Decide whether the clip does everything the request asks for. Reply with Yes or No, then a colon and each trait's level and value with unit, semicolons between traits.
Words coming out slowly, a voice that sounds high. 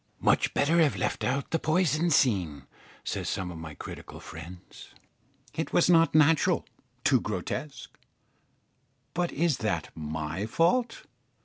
No: slow, 130 wpm; medium, 140 Hz